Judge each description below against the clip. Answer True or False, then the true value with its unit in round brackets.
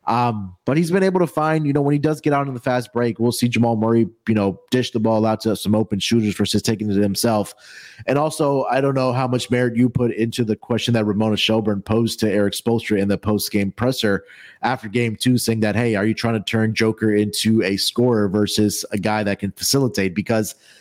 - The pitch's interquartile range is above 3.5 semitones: False (3.0 semitones)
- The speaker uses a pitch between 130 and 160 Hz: False (110 Hz)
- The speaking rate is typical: False (240 wpm)